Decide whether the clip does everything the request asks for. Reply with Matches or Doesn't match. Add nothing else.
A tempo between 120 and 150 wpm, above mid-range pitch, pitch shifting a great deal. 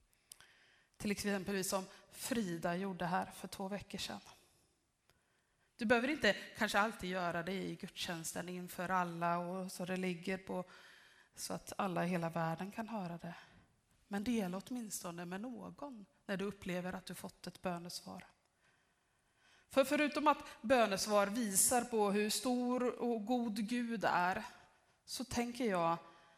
Doesn't match